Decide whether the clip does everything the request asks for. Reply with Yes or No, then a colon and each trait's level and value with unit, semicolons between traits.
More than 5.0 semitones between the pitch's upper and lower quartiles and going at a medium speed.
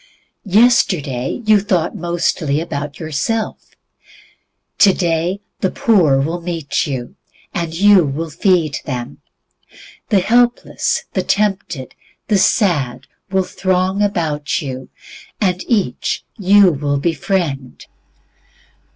No: wide, 5.4 semitones; slow, 100 wpm